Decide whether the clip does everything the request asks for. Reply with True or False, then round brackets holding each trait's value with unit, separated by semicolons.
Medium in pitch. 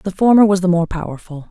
True (180 Hz)